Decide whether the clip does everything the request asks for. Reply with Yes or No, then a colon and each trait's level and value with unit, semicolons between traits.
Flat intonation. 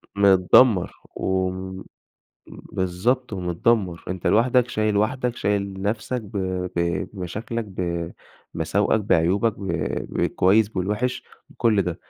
No: average, 3.7 semitones